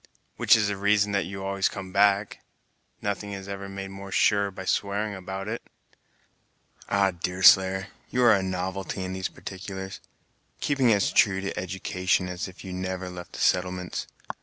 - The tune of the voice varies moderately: No, narrow, 1.4 semitones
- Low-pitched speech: Yes, very low, 95 Hz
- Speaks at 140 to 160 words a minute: No, average, 170 wpm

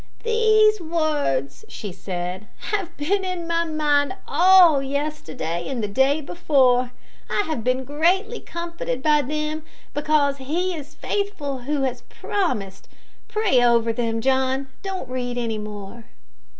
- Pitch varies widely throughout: Yes, wide, 5.8 semitones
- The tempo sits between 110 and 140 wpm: Yes, slow, 135 wpm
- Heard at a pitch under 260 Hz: No, very high, 285 Hz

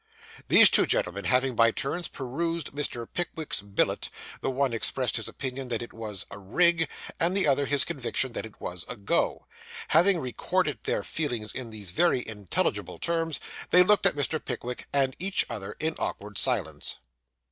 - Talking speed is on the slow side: No, average, 170 wpm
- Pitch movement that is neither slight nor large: No, wide, 6.3 semitones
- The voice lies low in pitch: Yes, low, 130 Hz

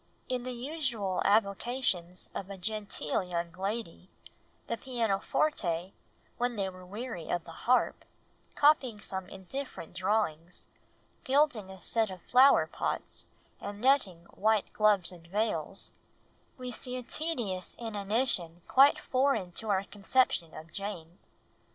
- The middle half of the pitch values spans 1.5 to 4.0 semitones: No, average, 5.2 semitones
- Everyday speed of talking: No, slow, 125 wpm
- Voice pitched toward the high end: Yes, high, 205 Hz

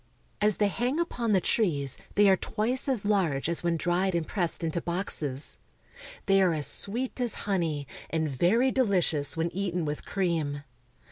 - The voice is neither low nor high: Yes, medium, 180 Hz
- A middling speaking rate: Yes, average, 175 wpm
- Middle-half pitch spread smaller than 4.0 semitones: No, average, 4.5 semitones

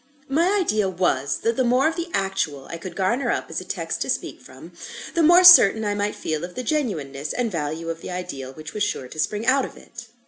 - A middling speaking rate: No, fast, 240 wpm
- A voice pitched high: Yes, high, 205 Hz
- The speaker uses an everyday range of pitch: No, wide, 8.0 semitones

